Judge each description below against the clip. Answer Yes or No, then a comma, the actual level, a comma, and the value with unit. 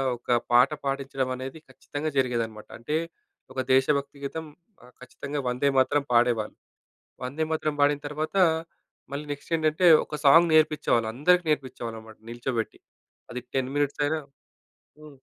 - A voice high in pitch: No, medium, 140 Hz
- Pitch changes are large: No, average, 3.3 semitones